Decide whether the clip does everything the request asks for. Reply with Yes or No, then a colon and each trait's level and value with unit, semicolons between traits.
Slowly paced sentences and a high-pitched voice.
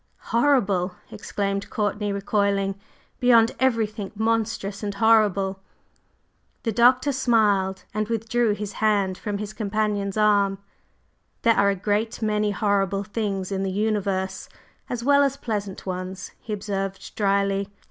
Yes: slow, 125 wpm; high, 205 Hz